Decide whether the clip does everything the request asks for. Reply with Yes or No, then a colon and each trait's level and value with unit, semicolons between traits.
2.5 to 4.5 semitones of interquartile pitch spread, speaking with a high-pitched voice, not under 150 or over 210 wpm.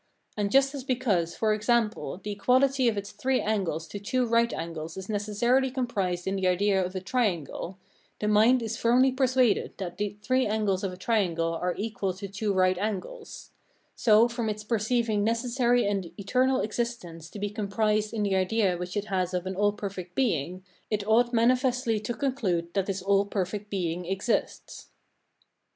Yes: average, 4.0 semitones; high, 210 Hz; average, 175 wpm